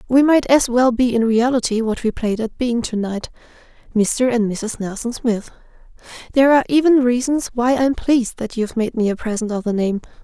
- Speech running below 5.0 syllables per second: No, 5.4 syllables/s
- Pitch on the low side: No, high, 235 Hz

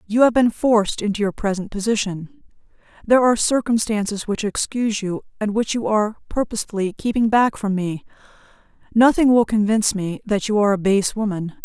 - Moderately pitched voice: No, high, 210 Hz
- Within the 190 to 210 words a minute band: No, average, 170 wpm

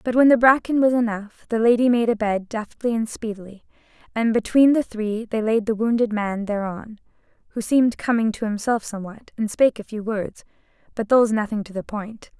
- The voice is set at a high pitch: Yes, high, 225 Hz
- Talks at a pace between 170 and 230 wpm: Yes, average, 200 wpm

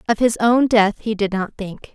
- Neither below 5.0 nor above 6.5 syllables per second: No, 4.6 syllables/s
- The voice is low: No, high, 215 Hz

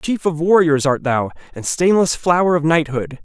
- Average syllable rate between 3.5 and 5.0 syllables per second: Yes, 4.8 syllables/s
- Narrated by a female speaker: No, male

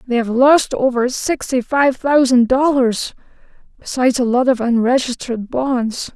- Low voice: No, very high, 255 Hz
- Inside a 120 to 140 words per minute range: Yes, slow, 135 wpm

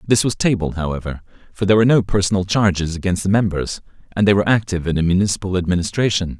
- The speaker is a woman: No, male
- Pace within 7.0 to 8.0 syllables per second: Yes, 7.2 syllables/s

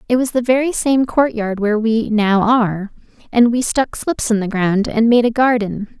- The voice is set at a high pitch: Yes, high, 230 Hz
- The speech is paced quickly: Yes, fast, 220 wpm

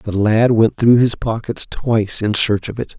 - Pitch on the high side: No, low, 110 Hz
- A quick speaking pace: Yes, fast, 220 wpm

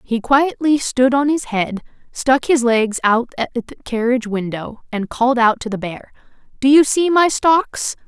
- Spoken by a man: No, female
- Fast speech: No, average, 185 wpm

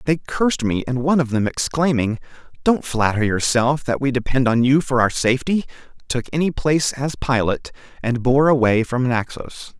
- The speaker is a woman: No, male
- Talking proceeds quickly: No, average, 180 wpm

